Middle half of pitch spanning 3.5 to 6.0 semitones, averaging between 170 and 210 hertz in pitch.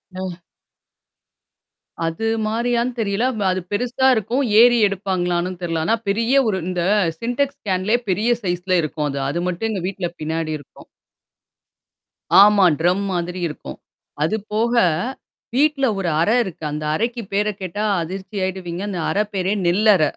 Yes: average, 4.3 semitones; high, 195 Hz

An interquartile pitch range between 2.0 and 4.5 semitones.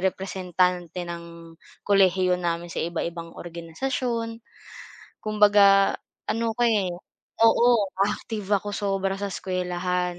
Yes: average, 2.9 semitones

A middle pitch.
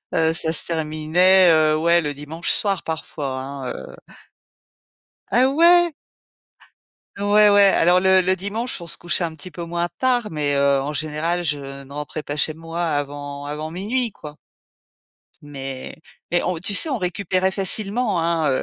Yes: medium, 165 Hz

